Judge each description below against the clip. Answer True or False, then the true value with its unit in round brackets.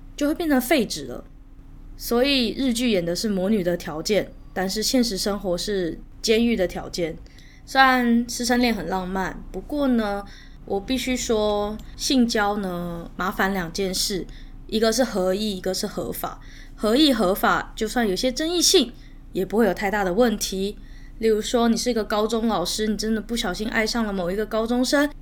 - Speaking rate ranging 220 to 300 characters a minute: True (260 characters per minute)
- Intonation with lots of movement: False (4.3 semitones)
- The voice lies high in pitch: True (215 Hz)